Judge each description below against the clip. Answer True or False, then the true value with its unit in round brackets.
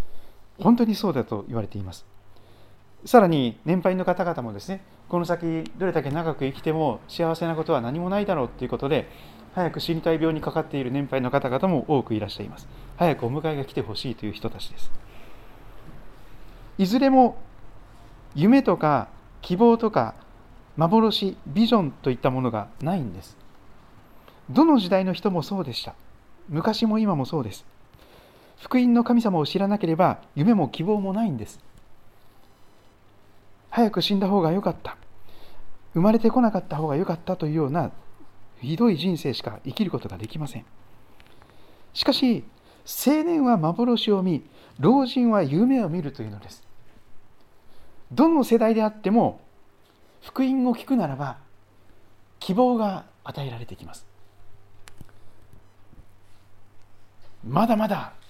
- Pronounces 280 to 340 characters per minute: True (285 characters per minute)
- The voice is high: False (140 Hz)